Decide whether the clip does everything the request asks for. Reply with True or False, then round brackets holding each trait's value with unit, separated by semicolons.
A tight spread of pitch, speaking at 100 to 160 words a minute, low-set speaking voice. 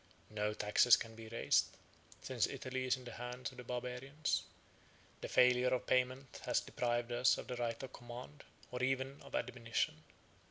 False (1.3 semitones; 170 wpm; 125 Hz)